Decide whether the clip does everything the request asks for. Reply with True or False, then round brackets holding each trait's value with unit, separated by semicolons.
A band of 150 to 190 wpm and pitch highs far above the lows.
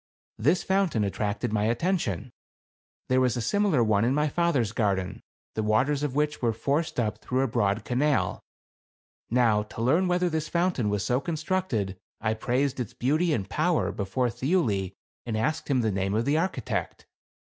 True (175 wpm; 6.1 semitones)